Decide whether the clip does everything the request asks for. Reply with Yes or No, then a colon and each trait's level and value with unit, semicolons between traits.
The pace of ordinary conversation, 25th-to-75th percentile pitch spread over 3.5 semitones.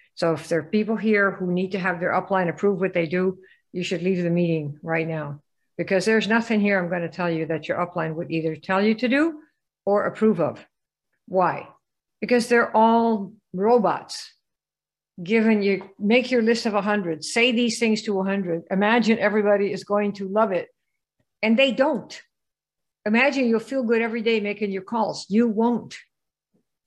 Yes: average, 185 wpm; average, 4.0 semitones